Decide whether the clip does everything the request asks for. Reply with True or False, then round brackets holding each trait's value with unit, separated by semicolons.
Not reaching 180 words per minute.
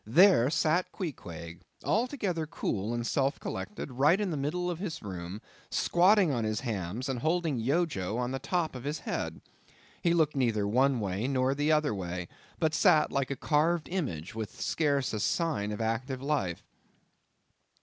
True (165 wpm)